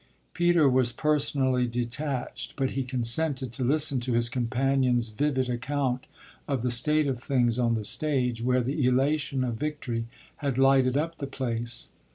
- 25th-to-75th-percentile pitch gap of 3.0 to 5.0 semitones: No, narrow, 2.6 semitones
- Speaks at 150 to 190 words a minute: Yes, average, 160 wpm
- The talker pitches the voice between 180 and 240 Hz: No, low, 130 Hz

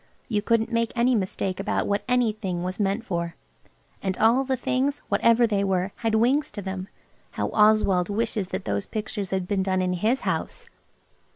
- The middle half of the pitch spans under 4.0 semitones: Yes, average, 3.5 semitones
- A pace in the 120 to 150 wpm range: No, average, 180 wpm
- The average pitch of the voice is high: Yes, high, 210 Hz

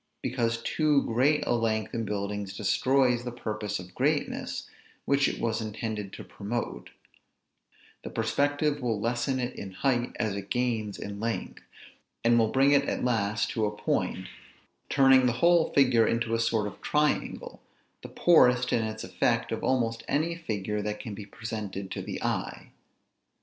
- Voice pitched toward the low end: Yes, low, 115 Hz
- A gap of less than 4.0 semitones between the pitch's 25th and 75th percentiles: Yes, average, 3.5 semitones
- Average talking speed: Yes, average, 165 wpm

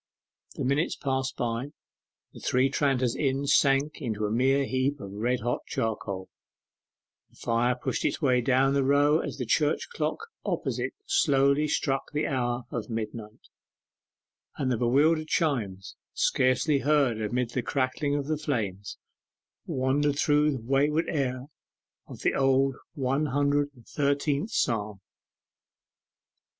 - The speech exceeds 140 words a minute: No, slow, 135 wpm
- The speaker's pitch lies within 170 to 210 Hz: No, low, 135 Hz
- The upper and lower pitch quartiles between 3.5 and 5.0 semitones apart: No, average, 2.9 semitones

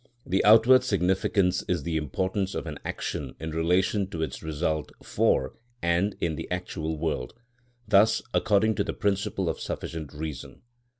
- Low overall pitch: Yes, very low, 90 Hz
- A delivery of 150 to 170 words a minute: Yes, average, 155 wpm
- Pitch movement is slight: No, average, 3.9 semitones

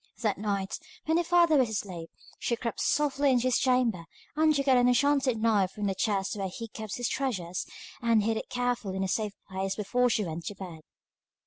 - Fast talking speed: Yes, fast, 210 wpm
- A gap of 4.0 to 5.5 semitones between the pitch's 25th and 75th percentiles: Yes, average, 4.8 semitones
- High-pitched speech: Yes, high, 225 Hz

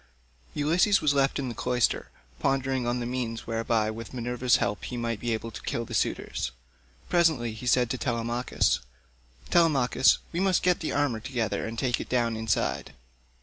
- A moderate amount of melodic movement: Yes, average, 3.0 semitones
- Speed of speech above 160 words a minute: Yes, average, 175 wpm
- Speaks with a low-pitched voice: Yes, low, 125 Hz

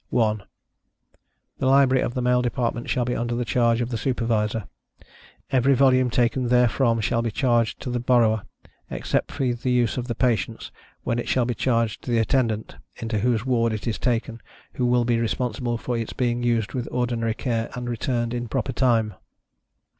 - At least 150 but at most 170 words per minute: No, average, 185 wpm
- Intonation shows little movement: Yes, narrow, 1.4 semitones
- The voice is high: No, low, 120 Hz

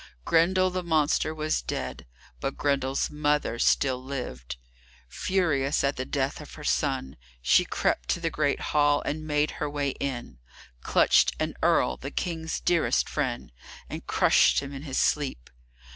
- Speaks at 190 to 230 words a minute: No, average, 155 wpm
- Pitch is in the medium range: Yes, medium, 145 Hz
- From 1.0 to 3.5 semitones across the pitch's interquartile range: Yes, average, 2.9 semitones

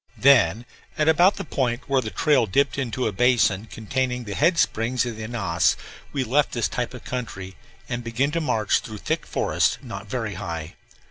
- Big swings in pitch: No, average, 4.0 semitones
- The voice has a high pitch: No, low, 125 Hz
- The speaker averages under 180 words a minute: No, average, 190 wpm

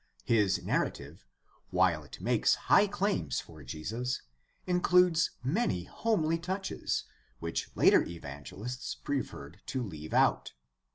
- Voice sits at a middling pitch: No, low, 115 Hz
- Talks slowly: Yes, slow, 110 wpm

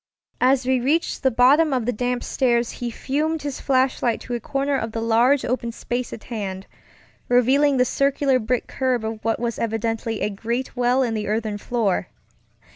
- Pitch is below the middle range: No, high, 245 Hz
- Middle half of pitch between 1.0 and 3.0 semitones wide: Yes, narrow, 2.6 semitones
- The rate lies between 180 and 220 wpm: Yes, average, 185 wpm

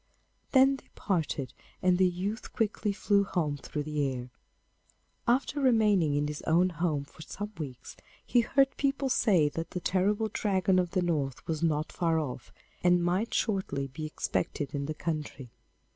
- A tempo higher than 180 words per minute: No, average, 165 wpm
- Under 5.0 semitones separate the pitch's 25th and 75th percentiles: No, wide, 5.5 semitones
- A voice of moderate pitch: Yes, medium, 175 Hz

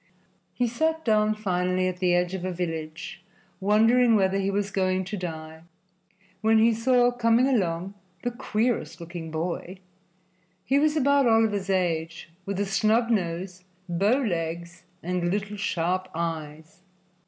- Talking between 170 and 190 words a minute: No, average, 140 wpm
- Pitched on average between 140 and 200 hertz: Yes, high, 190 Hz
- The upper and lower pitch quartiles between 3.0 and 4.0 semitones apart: No, average, 4.4 semitones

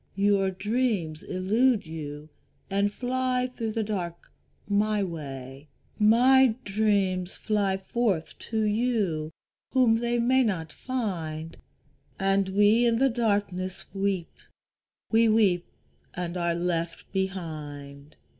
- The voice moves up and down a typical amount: Yes, average, 4.7 semitones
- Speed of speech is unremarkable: No, slow, 110 wpm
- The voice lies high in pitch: Yes, high, 200 Hz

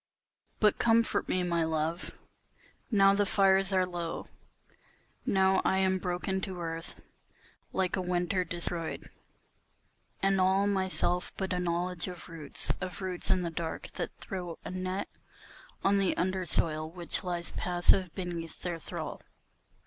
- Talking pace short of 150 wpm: Yes, average, 140 wpm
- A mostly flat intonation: Yes, narrow, 1.8 semitones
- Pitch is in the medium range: Yes, medium, 180 Hz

